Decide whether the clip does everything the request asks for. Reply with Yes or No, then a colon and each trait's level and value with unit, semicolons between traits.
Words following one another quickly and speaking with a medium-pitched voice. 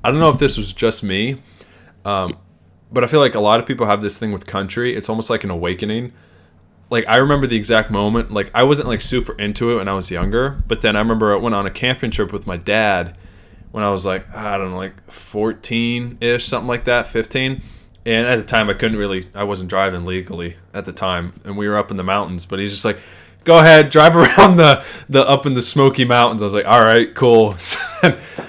No: fast, 235 wpm; low, 105 Hz